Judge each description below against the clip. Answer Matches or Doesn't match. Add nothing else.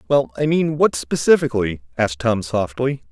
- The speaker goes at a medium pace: Doesn't match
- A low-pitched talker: Matches